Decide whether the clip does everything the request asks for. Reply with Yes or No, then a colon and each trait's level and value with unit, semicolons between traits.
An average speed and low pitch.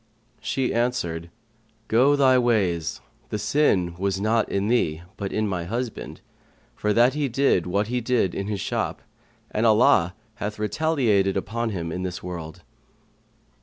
Yes: average, 150 wpm; low, 105 Hz